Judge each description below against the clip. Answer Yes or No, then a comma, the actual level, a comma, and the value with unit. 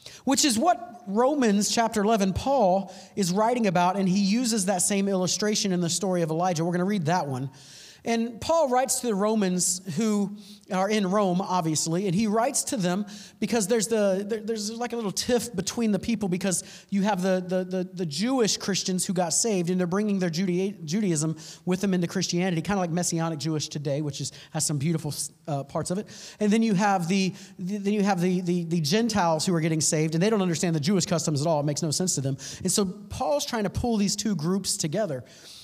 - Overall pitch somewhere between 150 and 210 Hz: Yes, high, 190 Hz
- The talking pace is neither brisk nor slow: No, fast, 220 wpm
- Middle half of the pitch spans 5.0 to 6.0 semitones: No, average, 3.3 semitones